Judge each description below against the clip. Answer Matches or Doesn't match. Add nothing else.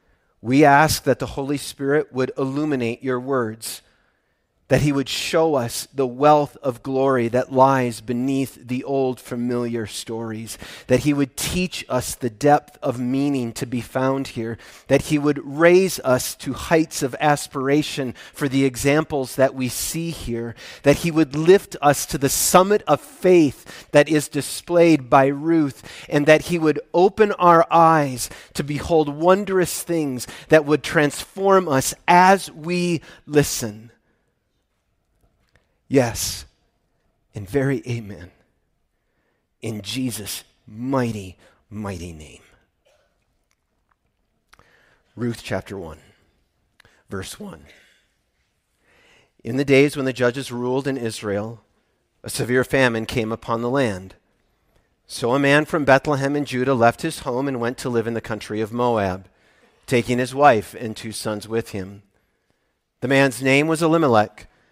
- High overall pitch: Doesn't match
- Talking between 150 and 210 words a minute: Doesn't match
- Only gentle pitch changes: Doesn't match